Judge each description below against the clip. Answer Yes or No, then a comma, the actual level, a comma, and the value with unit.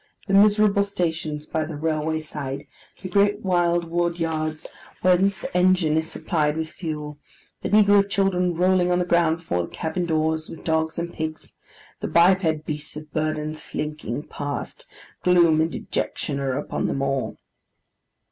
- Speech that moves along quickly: No, average, 155 wpm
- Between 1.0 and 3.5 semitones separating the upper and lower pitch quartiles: Yes, average, 2.7 semitones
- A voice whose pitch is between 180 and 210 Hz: No, medium, 160 Hz